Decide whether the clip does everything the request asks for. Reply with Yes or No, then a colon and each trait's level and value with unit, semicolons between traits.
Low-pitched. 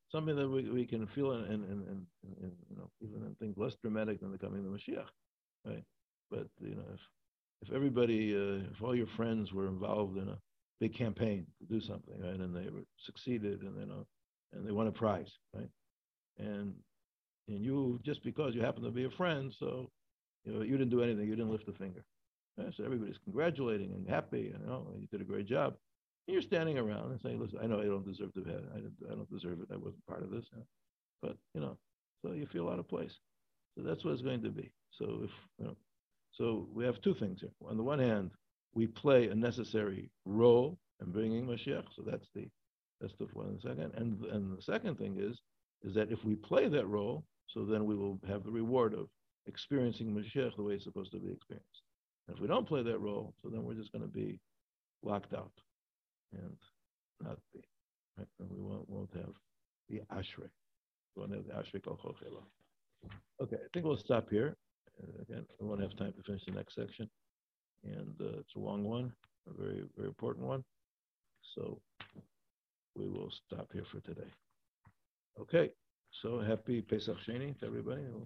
Yes: low, 110 Hz